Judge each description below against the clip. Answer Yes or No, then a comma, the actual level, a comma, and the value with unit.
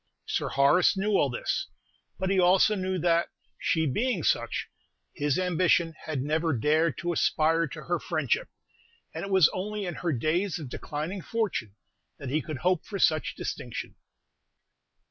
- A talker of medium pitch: Yes, medium, 165 Hz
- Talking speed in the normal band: Yes, average, 160 wpm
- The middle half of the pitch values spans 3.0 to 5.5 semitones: Yes, average, 3.5 semitones